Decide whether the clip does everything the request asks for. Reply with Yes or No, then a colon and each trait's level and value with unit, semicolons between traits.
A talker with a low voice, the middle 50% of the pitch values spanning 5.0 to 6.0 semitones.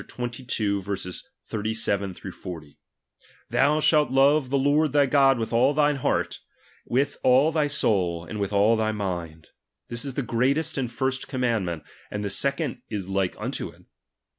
Yes: low, 120 Hz; wide, 5.6 semitones